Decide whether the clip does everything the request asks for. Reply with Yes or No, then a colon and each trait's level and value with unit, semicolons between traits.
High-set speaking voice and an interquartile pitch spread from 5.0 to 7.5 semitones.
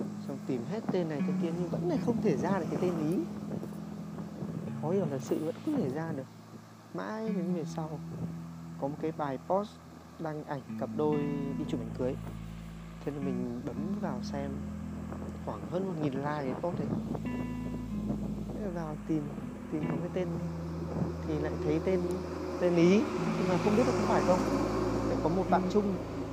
No: medium, 170 Hz; average, 5.3 semitones